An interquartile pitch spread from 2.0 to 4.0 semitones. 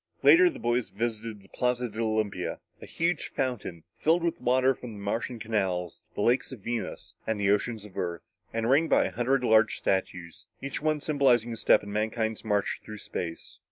Yes: average, 3.6 semitones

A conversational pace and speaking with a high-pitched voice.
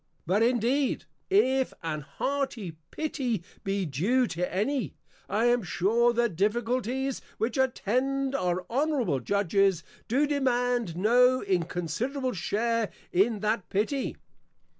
No: slow, 120 wpm; high, 230 Hz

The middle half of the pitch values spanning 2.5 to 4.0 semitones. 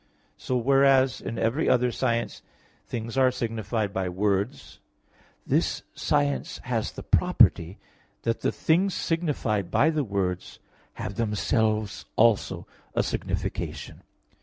No: average, 4.5 semitones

